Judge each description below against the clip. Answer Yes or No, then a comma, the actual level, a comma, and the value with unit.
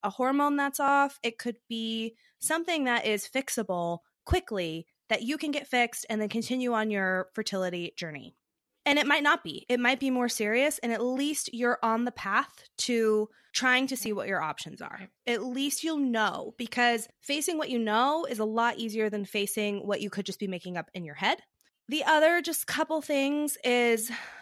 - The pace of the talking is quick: No, average, 195 wpm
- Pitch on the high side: Yes, high, 240 Hz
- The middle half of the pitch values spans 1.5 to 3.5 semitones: No, average, 4.6 semitones